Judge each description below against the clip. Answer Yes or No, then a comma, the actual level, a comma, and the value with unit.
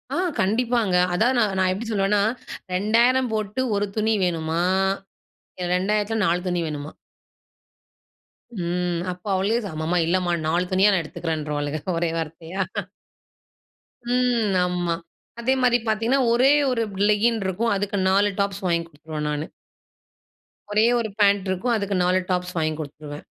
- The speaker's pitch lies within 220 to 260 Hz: No, high, 190 Hz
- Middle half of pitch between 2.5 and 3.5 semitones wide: No, average, 4.2 semitones